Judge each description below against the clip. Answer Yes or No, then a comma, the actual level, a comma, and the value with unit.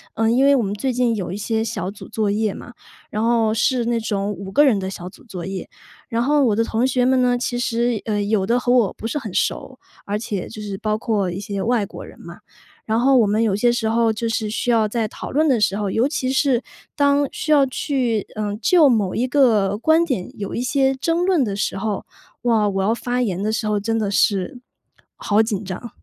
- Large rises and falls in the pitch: No, average, 3.3 semitones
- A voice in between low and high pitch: No, high, 225 Hz